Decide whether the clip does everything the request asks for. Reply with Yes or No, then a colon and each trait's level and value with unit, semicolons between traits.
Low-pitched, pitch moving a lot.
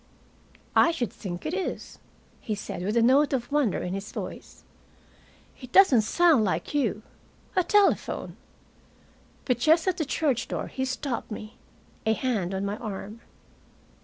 No: high, 245 Hz; wide, 5.8 semitones